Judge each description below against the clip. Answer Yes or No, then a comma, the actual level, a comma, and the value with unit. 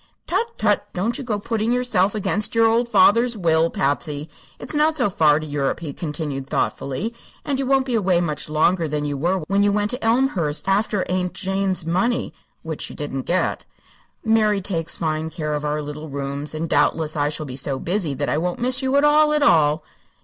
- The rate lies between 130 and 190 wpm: No, fast, 205 wpm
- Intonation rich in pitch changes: Yes, wide, 6.8 semitones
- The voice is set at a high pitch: No, medium, 180 Hz